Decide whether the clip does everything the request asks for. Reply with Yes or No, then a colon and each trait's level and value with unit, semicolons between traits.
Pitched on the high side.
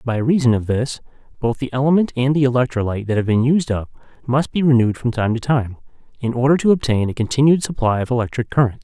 No: low, 125 Hz